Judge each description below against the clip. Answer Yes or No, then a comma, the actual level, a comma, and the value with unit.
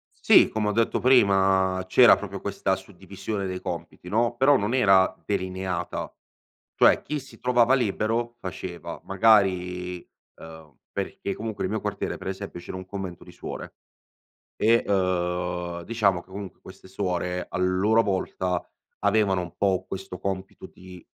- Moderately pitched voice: No, very low, 95 Hz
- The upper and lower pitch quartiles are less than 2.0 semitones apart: No, narrow, 2.5 semitones